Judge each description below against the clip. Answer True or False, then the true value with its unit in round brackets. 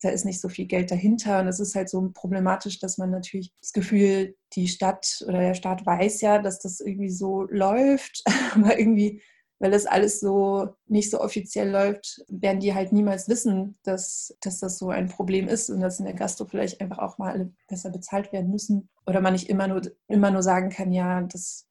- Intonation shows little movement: True (1.4 semitones)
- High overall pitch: True (195 Hz)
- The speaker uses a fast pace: True (215 wpm)